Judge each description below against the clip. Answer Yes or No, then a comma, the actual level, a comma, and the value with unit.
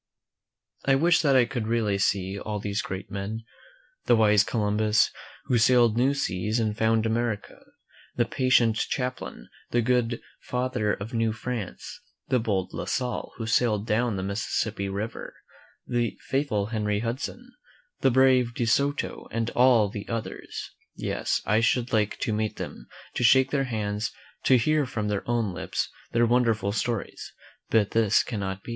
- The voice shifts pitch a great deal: No, average, 3.0 semitones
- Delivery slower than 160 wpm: No, average, 165 wpm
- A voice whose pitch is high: No, low, 115 Hz